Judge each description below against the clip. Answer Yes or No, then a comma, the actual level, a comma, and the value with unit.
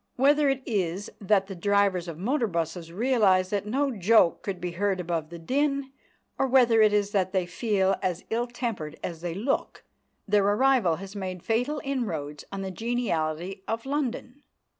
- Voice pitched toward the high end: Yes, high, 200 Hz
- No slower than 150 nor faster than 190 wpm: Yes, average, 175 wpm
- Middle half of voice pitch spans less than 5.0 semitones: No, average, 5.3 semitones